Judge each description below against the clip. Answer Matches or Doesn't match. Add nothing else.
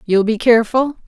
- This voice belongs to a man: Doesn't match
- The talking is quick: Doesn't match